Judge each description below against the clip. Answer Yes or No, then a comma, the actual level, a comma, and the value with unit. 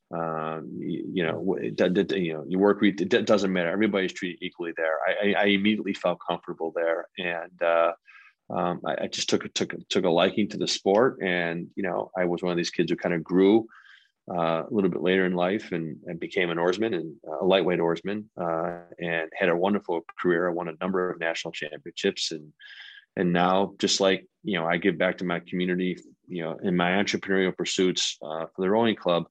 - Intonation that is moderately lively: No, narrow, 2.1 semitones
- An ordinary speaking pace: No, fast, 210 wpm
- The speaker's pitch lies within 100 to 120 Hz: No, very low, 90 Hz